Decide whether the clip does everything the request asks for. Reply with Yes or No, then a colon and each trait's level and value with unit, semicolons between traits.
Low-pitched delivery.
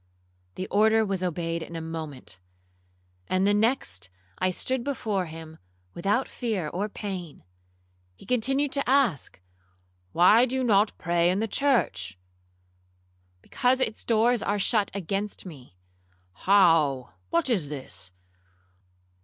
No: medium, 185 Hz